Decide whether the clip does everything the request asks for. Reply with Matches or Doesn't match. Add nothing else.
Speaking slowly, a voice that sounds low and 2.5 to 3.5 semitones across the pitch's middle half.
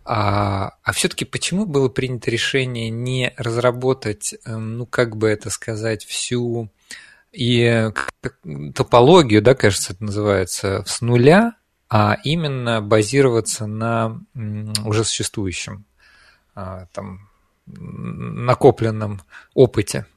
Matches